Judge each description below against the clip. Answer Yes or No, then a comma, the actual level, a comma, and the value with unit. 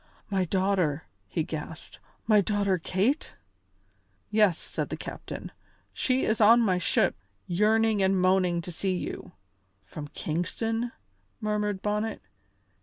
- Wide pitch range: No, average, 3.1 semitones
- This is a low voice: No, high, 195 Hz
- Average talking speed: No, slow, 120 wpm